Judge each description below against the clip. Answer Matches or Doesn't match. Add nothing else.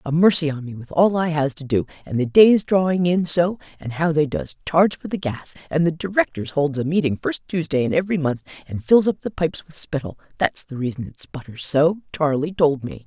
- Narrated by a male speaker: Doesn't match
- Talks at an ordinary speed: Doesn't match